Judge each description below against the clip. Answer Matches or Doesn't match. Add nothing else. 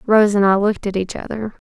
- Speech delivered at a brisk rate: Matches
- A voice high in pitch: Matches